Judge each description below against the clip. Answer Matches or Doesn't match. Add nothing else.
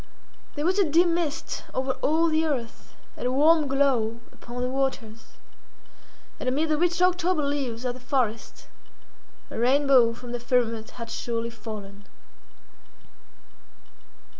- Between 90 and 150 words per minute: Matches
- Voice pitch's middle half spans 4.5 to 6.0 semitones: Matches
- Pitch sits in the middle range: Doesn't match